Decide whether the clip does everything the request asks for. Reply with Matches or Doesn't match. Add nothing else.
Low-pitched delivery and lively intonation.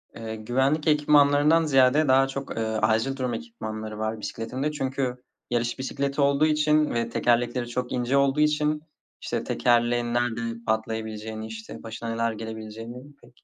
Doesn't match